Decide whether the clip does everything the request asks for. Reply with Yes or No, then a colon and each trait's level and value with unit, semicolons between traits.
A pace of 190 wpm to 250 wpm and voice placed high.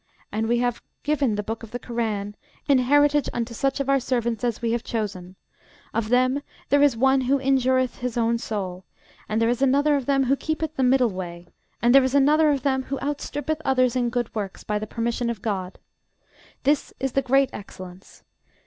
Yes: fast, 205 wpm; high, 245 Hz